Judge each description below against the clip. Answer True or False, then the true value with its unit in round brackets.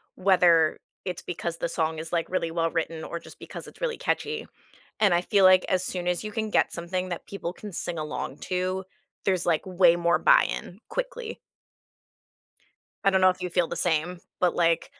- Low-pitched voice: False (180 Hz)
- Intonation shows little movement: True (2.1 semitones)